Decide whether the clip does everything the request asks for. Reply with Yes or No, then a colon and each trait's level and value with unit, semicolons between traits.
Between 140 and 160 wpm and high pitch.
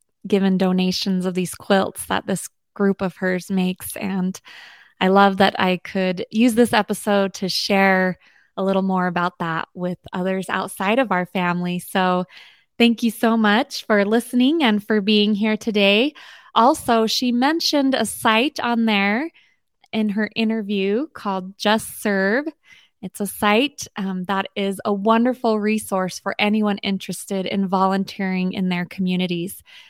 Yes: average, 150 wpm; high, 200 Hz